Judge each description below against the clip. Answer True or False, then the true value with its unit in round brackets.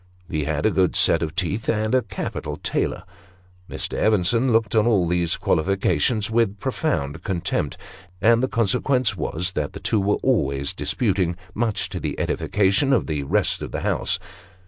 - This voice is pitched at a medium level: False (100 Hz)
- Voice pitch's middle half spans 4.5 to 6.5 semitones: True (5.1 semitones)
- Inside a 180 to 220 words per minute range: False (170 wpm)